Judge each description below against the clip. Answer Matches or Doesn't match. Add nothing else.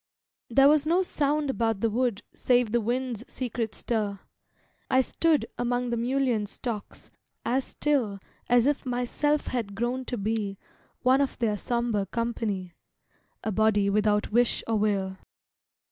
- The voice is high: Matches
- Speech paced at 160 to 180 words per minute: Doesn't match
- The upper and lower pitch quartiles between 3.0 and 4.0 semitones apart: Matches